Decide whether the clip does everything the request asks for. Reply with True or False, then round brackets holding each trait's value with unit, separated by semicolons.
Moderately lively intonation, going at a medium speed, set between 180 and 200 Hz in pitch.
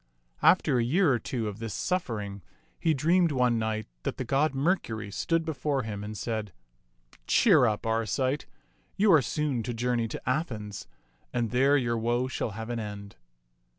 False (4.5 semitones; 175 wpm; 120 Hz)